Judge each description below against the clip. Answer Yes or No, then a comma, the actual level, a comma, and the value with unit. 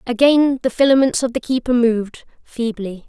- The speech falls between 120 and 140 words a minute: Yes, slow, 135 wpm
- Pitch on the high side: Yes, high, 245 Hz